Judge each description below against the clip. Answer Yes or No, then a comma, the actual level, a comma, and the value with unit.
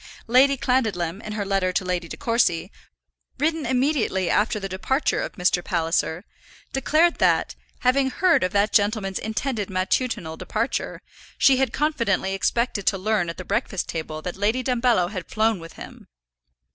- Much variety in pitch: Yes, wide, 5.7 semitones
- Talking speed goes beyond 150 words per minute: Yes, average, 160 wpm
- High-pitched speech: Yes, high, 210 Hz